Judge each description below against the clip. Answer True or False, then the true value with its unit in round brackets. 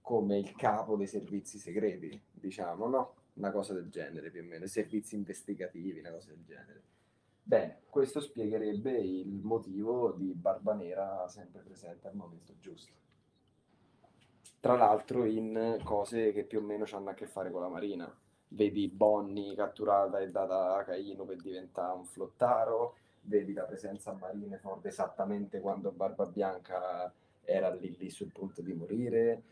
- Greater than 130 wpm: True (155 wpm)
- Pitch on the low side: True (100 Hz)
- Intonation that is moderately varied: False (2.0 semitones)